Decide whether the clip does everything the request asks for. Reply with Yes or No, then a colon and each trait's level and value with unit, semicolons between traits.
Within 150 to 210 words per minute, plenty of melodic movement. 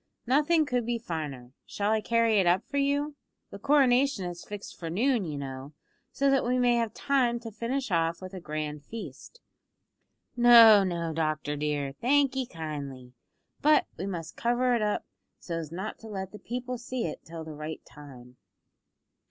Yes: average, 175 wpm; wide, 7.7 semitones